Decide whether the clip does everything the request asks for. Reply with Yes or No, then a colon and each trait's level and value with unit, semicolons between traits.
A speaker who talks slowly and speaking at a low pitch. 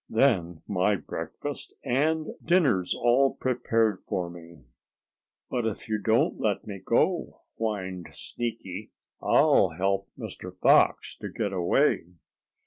Yes: slow, 120 wpm; low, 105 Hz